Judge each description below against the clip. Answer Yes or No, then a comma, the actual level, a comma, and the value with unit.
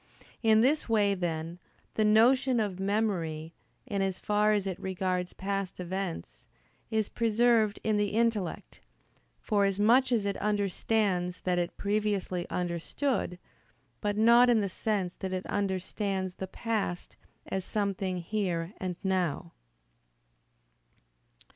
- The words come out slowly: Yes, slow, 125 wpm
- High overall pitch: Yes, high, 200 Hz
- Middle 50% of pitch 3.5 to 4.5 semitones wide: No, average, 2.9 semitones